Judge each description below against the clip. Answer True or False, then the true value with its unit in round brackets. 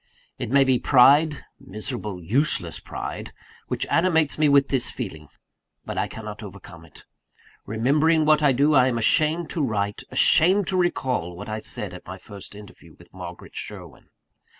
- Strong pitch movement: True (6.5 semitones)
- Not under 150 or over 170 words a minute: True (165 wpm)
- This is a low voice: True (130 Hz)